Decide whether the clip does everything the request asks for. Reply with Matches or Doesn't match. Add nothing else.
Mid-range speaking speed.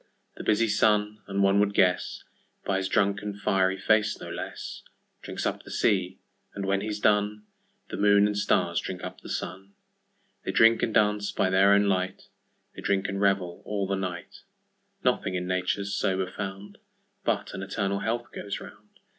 Matches